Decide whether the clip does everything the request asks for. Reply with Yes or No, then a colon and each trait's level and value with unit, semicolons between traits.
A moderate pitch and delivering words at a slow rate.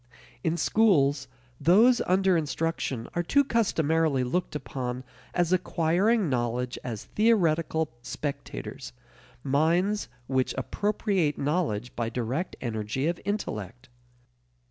Yes: medium, 155 Hz; slow, 100 wpm